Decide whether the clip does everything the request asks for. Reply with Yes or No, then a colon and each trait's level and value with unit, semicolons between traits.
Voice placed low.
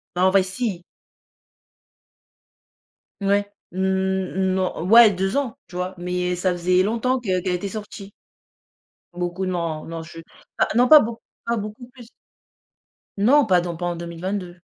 No: high, 190 Hz